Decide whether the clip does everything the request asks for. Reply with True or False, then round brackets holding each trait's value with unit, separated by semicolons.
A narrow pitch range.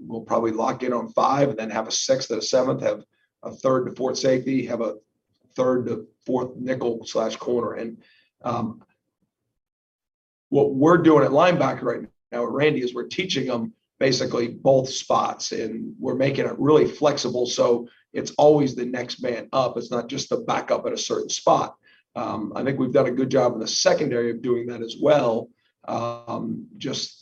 True (2.0 semitones)